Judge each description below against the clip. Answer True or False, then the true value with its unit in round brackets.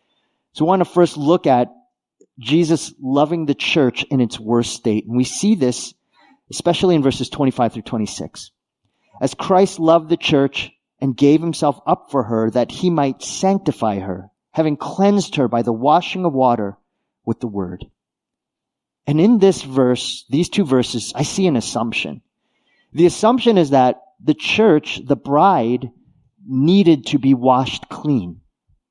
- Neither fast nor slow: True (160 wpm)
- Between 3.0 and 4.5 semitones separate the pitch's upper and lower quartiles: False (5.5 semitones)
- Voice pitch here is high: False (140 Hz)